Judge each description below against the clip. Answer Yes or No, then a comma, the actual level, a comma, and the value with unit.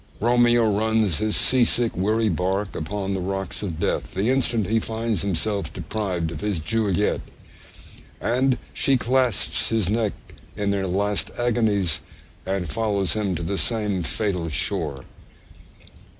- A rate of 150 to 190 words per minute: No, average, 140 wpm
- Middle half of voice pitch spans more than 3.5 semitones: No, average, 3.2 semitones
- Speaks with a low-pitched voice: Yes, low, 105 Hz